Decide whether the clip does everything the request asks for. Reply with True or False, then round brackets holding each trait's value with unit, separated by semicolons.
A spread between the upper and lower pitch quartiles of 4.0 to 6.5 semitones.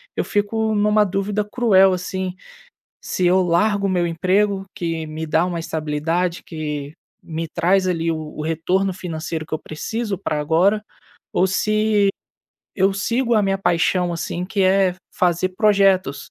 False (3.3 semitones)